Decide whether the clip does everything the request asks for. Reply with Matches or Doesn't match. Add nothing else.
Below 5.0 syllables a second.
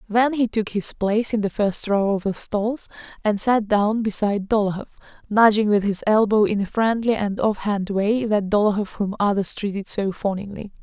Doesn't match